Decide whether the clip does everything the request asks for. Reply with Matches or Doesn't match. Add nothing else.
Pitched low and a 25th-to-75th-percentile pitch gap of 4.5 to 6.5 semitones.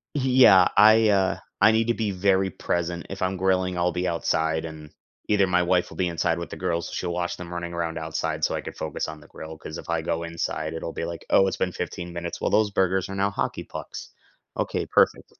Doesn't match